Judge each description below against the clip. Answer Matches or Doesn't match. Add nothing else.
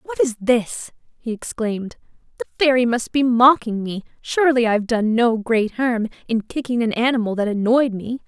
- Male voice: Doesn't match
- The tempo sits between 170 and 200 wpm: Matches